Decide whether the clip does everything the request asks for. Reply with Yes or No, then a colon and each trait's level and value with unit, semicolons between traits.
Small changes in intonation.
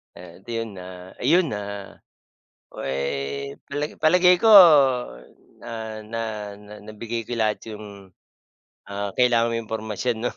No: average, 3.3 semitones